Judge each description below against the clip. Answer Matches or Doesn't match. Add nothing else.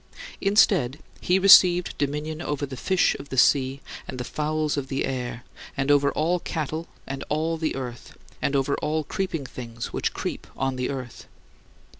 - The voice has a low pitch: Doesn't match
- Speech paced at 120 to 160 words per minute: Doesn't match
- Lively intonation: Doesn't match